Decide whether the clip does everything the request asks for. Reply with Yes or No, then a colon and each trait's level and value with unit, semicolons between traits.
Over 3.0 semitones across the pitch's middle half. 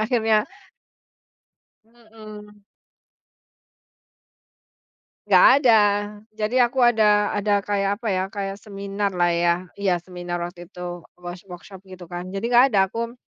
Yes: average, 3.5 semitones